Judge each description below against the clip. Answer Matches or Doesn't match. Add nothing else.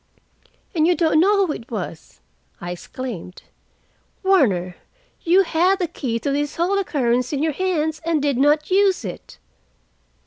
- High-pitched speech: Matches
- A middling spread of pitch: Doesn't match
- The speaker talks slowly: Doesn't match